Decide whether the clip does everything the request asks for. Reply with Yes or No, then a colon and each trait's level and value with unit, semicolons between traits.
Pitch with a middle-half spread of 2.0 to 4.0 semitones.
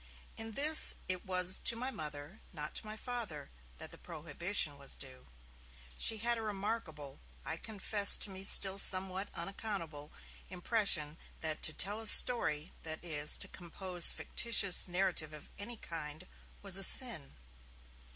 No: average, 5.3 semitones